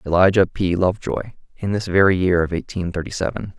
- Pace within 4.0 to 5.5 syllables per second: No, 5.8 syllables/s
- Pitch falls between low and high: No, very low, 95 Hz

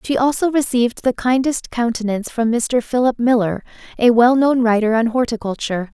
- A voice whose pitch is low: No, high, 240 Hz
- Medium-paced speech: Yes, average, 150 wpm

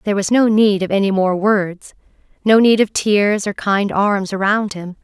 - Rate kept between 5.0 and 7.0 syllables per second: No, 4.6 syllables/s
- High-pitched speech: Yes, high, 200 Hz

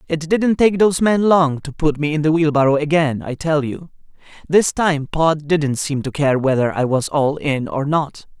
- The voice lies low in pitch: No, medium, 150 Hz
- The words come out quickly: Yes, fast, 215 wpm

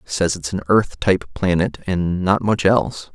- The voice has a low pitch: Yes, very low, 90 Hz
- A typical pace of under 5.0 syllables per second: Yes, 4.6 syllables/s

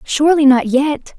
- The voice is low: No, very high, 285 Hz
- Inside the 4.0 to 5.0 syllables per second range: Yes, 4.6 syllables/s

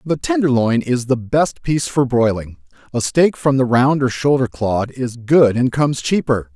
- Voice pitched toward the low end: Yes, low, 130 Hz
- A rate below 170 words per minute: No, average, 190 wpm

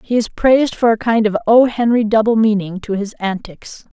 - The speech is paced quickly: Yes, fast, 210 wpm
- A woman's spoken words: Yes, female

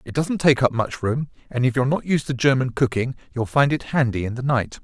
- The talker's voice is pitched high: No, low, 130 Hz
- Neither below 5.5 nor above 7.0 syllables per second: Yes, 5.8 syllables/s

